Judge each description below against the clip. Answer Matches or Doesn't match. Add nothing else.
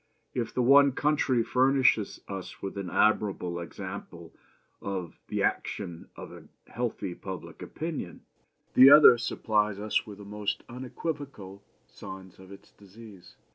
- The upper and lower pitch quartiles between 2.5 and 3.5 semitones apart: Doesn't match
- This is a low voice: Matches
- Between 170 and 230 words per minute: Doesn't match